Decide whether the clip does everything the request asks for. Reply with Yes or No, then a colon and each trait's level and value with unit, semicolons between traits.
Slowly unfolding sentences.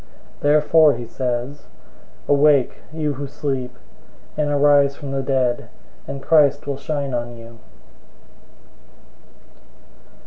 Yes: slow, 110 wpm